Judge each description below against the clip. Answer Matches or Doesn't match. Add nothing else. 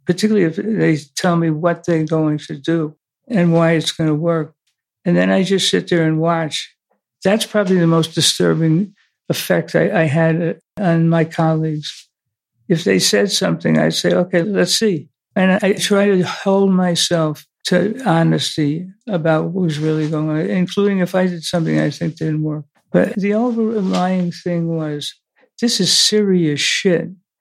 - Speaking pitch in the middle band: Matches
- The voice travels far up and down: Doesn't match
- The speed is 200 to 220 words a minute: Doesn't match